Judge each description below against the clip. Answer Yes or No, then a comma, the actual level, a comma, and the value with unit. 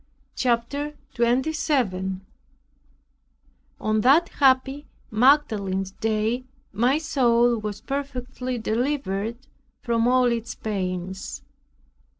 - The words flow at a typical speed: No, slow, 80 wpm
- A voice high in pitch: Yes, high, 235 Hz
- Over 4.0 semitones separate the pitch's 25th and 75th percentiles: No, average, 3.7 semitones